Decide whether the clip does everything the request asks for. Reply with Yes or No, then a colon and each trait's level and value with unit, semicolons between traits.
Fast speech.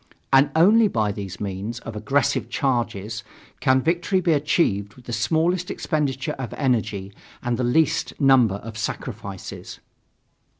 No: slow, 135 wpm